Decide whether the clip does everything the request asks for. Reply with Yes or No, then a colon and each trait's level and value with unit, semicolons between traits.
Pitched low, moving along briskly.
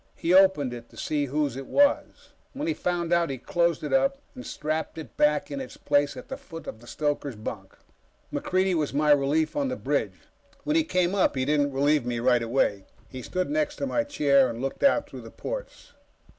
No: medium, 150 Hz; fast, 215 wpm